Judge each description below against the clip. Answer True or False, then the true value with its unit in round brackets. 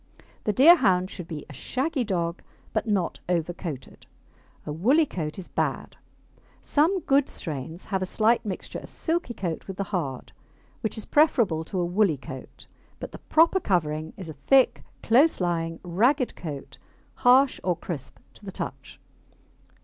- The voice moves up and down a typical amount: False (7.2 semitones)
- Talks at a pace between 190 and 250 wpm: False (160 wpm)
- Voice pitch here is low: False (185 Hz)